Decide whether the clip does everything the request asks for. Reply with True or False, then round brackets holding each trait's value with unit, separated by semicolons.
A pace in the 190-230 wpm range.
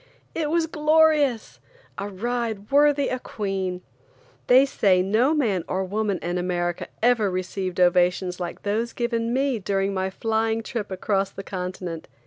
False (145 wpm)